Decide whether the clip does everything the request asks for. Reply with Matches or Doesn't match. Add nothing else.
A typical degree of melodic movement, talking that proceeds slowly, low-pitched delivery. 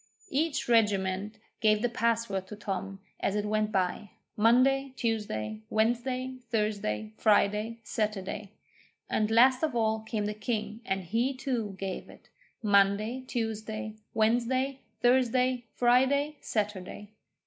Doesn't match